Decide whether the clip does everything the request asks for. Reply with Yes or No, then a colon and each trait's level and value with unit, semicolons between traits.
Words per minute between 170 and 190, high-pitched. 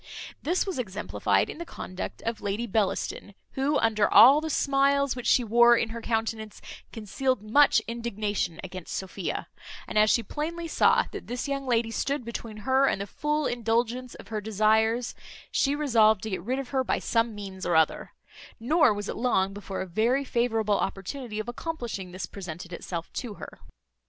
Yes: average, 180 wpm; high, 230 Hz